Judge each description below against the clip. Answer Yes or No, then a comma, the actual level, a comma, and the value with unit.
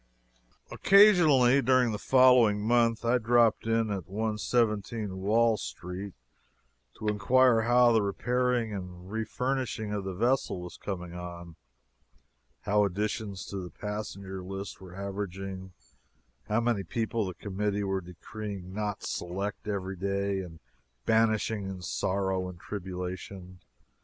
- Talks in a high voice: No, low, 105 Hz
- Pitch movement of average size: Yes, average, 3.3 semitones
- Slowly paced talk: Yes, slow, 125 wpm